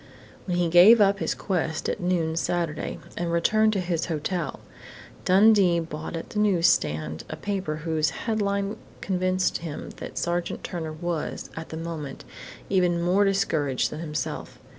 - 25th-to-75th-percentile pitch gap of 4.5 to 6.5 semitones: No, average, 3.2 semitones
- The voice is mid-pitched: Yes, medium, 175 Hz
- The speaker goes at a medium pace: Yes, average, 150 wpm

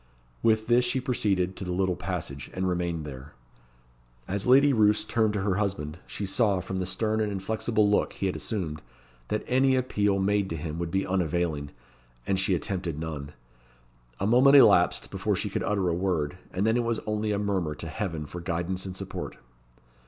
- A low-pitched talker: Yes, very low, 95 Hz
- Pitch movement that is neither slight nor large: Yes, average, 3.7 semitones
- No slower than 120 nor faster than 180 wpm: No, average, 190 wpm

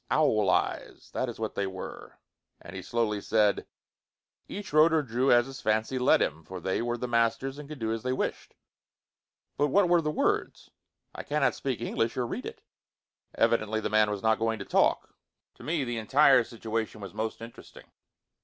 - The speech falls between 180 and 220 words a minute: Yes, average, 190 wpm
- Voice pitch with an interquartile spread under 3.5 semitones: No, average, 3.8 semitones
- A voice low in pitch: Yes, low, 115 Hz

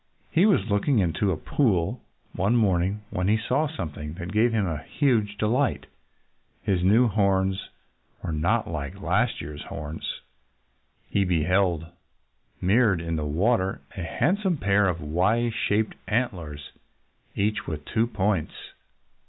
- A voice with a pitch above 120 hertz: No, low, 100 Hz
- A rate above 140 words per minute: No, slow, 135 wpm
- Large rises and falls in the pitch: No, average, 4.8 semitones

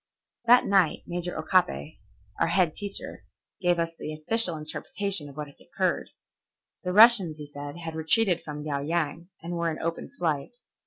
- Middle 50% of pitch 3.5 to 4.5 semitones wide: No, average, 3.1 semitones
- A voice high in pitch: No, medium, 165 Hz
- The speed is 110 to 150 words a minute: No, average, 165 wpm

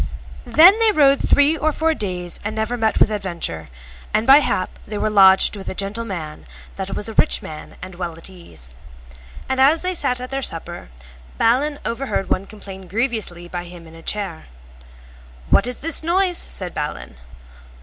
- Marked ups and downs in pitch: Yes, wide, 7.4 semitones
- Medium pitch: No, high, 210 Hz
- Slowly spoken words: No, average, 180 wpm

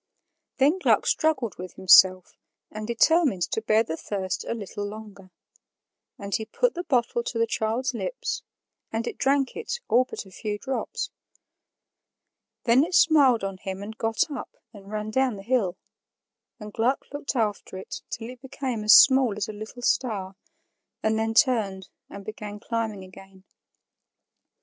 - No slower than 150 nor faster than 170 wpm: Yes, average, 160 wpm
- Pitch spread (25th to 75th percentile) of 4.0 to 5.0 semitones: Yes, average, 4.3 semitones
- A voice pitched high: Yes, high, 220 Hz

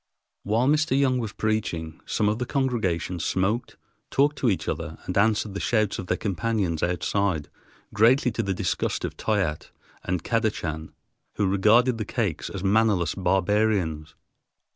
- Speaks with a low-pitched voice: Yes, low, 105 Hz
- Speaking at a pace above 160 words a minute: No, average, 150 wpm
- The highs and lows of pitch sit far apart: No, average, 4.2 semitones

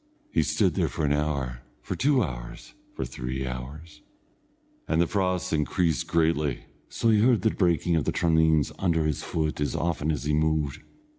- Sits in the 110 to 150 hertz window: No, very low, 80 Hz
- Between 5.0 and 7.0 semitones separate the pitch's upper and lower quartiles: No, average, 3.1 semitones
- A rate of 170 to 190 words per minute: Yes, average, 180 wpm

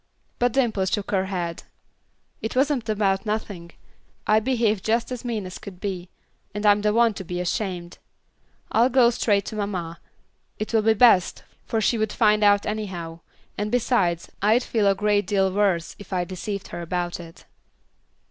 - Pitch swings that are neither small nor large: Yes, average, 3.2 semitones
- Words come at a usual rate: Yes, average, 175 wpm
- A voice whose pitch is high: Yes, high, 205 Hz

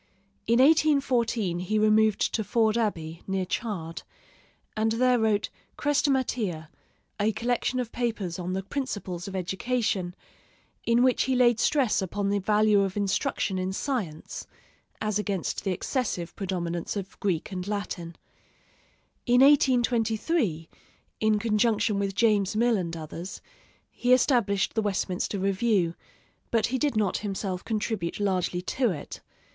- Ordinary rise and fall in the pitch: Yes, average, 4.0 semitones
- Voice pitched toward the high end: Yes, high, 210 Hz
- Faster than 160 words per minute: No, slow, 135 wpm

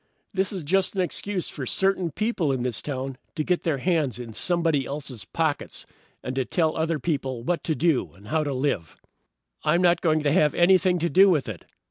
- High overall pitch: No, medium, 155 Hz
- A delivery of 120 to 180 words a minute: No, fast, 205 wpm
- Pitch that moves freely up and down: No, average, 4.8 semitones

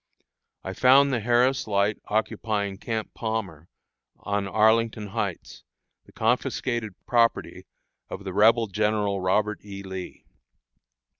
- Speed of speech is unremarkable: No, slow, 115 wpm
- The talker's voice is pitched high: No, low, 105 Hz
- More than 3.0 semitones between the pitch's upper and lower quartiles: No, narrow, 2.6 semitones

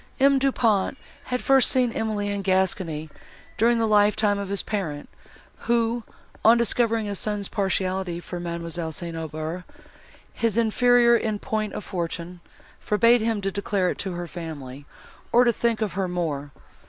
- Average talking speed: Yes, average, 160 wpm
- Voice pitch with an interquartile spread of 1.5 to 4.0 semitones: No, average, 4.7 semitones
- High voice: Yes, high, 200 Hz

